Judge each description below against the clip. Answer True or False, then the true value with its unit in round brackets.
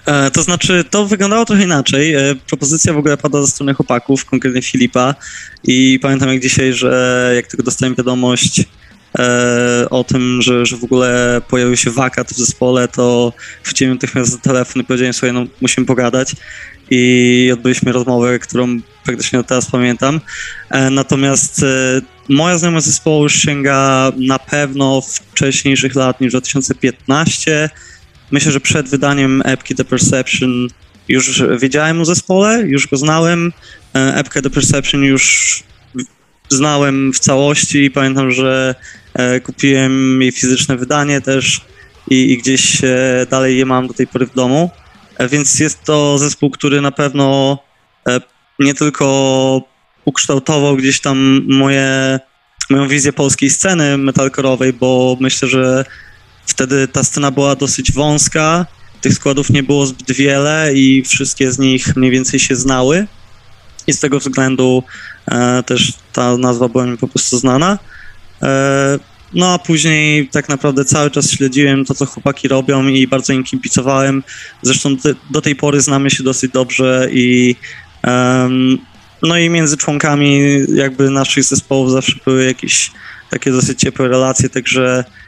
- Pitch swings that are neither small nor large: False (1.8 semitones)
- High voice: False (135 Hz)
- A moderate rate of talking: True (150 wpm)